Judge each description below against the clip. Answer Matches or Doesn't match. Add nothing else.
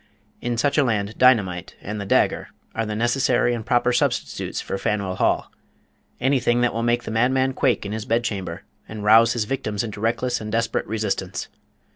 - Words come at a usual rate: Matches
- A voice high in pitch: Doesn't match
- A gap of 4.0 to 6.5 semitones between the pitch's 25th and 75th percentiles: Doesn't match